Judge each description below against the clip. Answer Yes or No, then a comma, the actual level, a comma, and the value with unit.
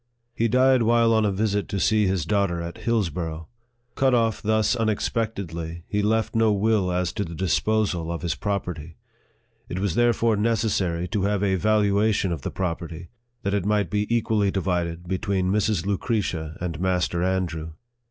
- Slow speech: No, average, 170 wpm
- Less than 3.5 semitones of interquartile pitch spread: No, average, 3.9 semitones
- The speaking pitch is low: Yes, low, 100 Hz